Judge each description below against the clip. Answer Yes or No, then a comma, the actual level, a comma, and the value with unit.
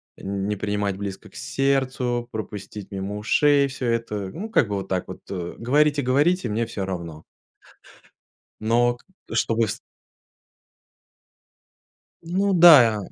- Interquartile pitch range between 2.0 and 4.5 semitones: No, wide, 5.4 semitones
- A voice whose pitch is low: Yes, low, 115 Hz